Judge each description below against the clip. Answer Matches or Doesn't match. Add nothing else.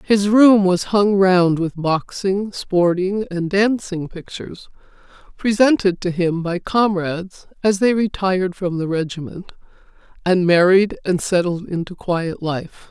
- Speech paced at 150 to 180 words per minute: Doesn't match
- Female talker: Matches